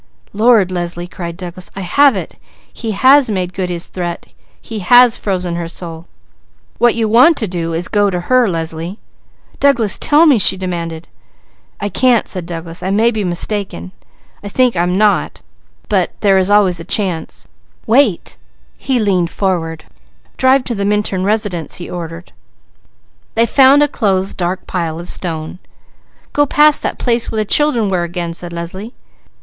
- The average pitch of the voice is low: No, high, 190 Hz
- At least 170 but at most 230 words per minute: No, average, 160 wpm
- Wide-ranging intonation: No, average, 4.7 semitones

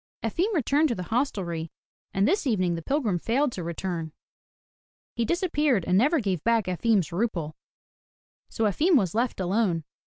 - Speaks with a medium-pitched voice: No, high, 215 Hz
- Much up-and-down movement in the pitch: Yes, wide, 7.0 semitones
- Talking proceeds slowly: No, average, 155 wpm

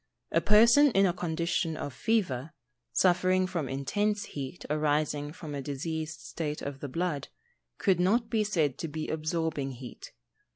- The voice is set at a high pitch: No, medium, 160 Hz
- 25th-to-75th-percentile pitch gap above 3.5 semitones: Yes, average, 4.1 semitones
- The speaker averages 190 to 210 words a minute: No, average, 155 wpm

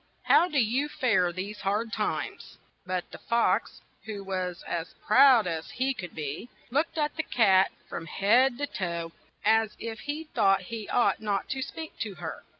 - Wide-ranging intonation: Yes, wide, 6.0 semitones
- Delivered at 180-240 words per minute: Yes, average, 185 wpm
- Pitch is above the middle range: Yes, high, 215 Hz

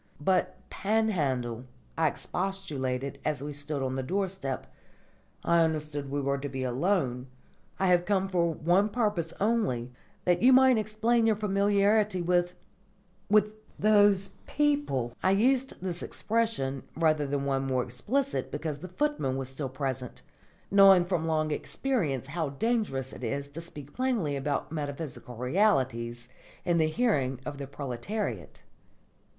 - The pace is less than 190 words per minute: Yes, average, 140 wpm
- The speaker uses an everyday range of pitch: No, wide, 7.0 semitones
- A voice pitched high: No, medium, 160 Hz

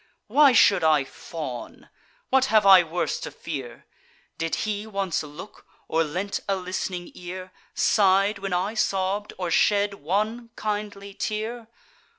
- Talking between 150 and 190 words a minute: No, average, 140 wpm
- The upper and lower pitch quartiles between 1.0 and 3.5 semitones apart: Yes, average, 3.1 semitones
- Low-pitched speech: No, high, 195 Hz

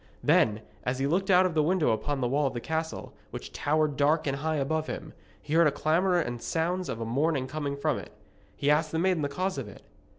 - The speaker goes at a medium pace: No, fast, 240 wpm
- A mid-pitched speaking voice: Yes, medium, 155 Hz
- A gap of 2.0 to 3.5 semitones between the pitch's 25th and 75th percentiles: Yes, average, 3.0 semitones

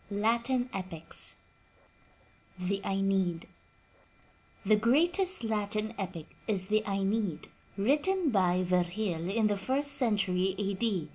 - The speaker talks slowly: Yes, slow, 110 wpm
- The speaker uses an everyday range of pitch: Yes, average, 3.7 semitones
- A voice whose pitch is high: Yes, high, 200 Hz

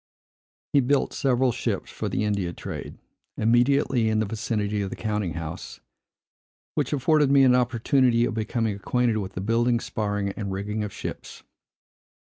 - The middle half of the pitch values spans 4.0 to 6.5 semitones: No, average, 3.3 semitones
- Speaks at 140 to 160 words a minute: Yes, average, 155 wpm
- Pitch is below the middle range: Yes, low, 110 Hz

